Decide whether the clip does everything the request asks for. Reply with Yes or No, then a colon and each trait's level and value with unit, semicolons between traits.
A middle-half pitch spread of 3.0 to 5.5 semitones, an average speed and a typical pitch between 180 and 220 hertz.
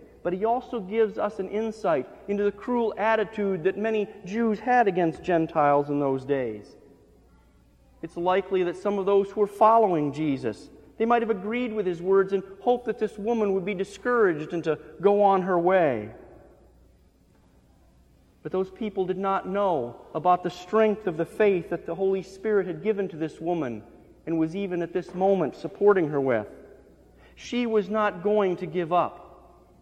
Yes: average, 4.1 semitones; average, 175 wpm; high, 190 Hz